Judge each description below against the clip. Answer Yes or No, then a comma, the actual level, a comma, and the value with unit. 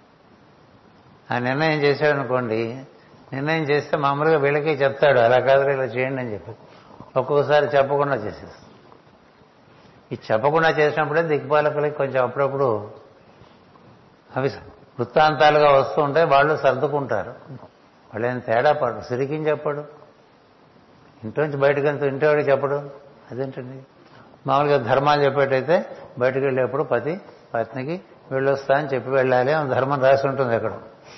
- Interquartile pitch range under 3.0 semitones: Yes, narrow, 2.4 semitones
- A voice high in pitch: No, medium, 140 Hz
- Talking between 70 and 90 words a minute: No, average, 110 wpm